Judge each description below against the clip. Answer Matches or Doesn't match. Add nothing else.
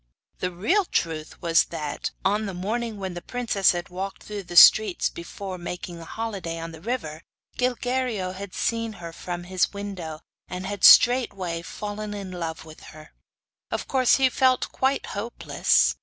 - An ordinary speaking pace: Matches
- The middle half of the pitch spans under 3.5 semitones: Doesn't match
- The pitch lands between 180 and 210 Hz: Matches